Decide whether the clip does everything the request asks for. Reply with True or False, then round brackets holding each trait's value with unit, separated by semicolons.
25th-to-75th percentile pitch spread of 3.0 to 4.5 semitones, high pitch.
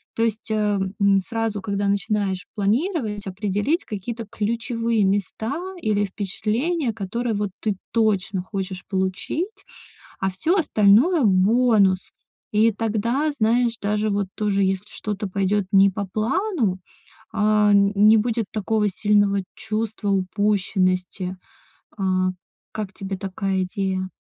False (2.5 semitones; 210 Hz)